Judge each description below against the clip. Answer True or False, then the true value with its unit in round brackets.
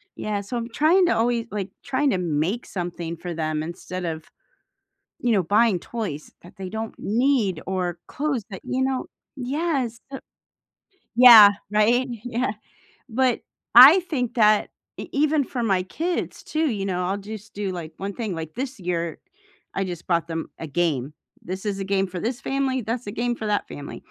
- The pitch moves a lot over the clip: True (5.7 semitones)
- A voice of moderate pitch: False (210 Hz)